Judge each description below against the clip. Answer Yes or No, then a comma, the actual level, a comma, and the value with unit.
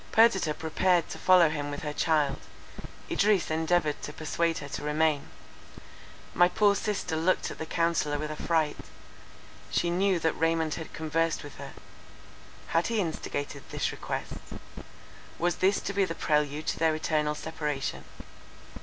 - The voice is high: No, medium, 160 Hz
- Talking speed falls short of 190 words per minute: Yes, average, 145 wpm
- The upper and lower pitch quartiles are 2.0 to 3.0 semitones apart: Yes, average, 2.7 semitones